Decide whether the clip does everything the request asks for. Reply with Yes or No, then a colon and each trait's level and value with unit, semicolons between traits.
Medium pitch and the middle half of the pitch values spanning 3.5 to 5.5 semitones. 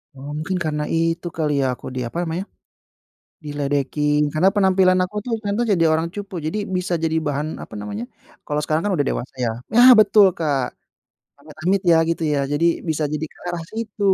Yes: medium, 160 Hz; average, 4.3 semitones